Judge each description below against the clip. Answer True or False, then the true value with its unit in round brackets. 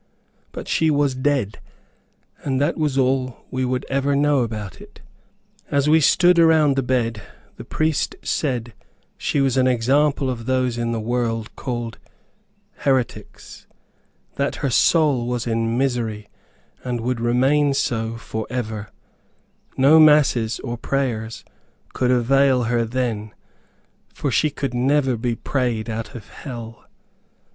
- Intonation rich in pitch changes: False (3.2 semitones)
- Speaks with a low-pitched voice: True (125 Hz)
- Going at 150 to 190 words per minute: False (135 wpm)